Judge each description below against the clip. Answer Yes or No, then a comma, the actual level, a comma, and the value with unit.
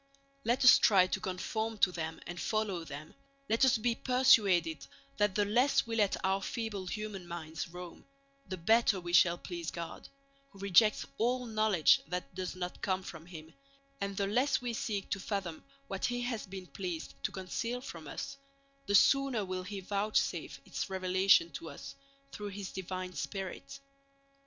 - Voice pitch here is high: Yes, high, 195 Hz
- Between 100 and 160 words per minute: No, average, 170 wpm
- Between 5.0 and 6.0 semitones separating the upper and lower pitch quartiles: No, average, 3.7 semitones